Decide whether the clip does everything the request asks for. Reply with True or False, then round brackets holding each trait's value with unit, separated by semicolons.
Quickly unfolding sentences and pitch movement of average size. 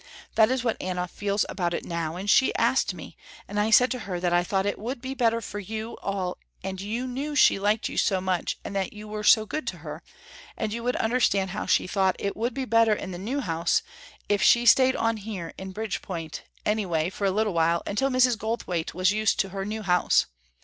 True (230 wpm; 3.5 semitones)